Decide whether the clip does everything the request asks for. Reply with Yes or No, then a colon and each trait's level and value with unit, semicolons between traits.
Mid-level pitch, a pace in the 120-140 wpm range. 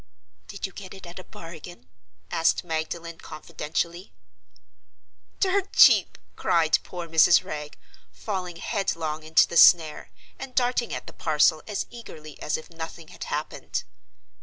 Yes: medium, 170 Hz; slow, 135 wpm